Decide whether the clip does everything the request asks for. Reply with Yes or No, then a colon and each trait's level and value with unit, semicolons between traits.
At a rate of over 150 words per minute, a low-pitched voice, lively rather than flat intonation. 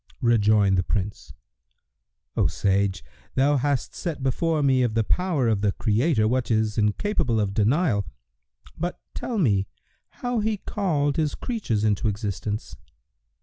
No: average, 140 wpm; low, 115 Hz; wide, 6.7 semitones